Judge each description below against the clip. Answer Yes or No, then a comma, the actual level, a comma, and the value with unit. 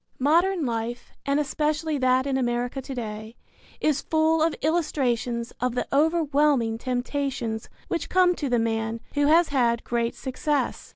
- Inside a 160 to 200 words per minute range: No, average, 150 wpm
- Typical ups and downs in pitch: Yes, average, 4.1 semitones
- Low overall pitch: No, very high, 265 Hz